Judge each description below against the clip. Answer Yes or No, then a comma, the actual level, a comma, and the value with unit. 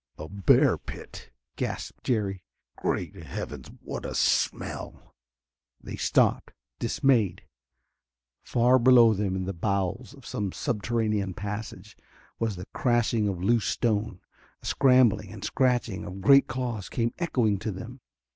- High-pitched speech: No, low, 110 Hz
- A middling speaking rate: No, slow, 130 wpm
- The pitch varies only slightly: No, average, 3.7 semitones